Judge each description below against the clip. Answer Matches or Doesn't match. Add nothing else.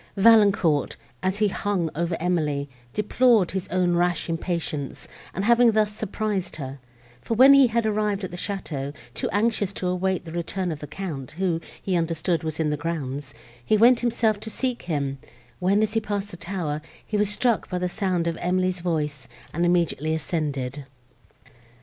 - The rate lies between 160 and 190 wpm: Matches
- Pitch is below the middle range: Doesn't match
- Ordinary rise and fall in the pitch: Matches